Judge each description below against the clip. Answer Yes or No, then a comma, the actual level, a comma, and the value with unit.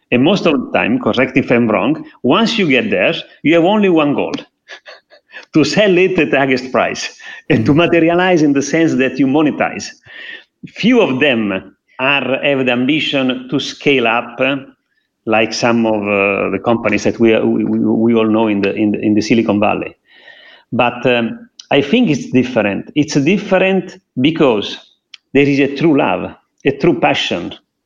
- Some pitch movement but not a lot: No, wide, 7.1 semitones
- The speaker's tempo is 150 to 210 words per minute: Yes, average, 180 wpm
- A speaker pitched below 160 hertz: Yes, low, 135 Hz